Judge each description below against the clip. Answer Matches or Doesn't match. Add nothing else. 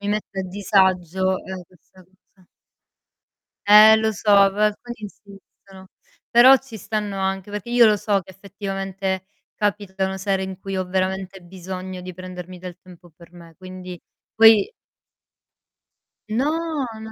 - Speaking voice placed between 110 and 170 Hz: Doesn't match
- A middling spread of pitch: Doesn't match